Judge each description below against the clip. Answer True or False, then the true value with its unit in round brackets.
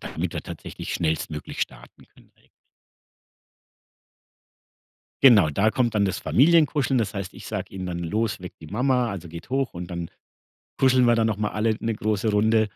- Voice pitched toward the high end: False (105 Hz)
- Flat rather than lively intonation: False (4.9 semitones)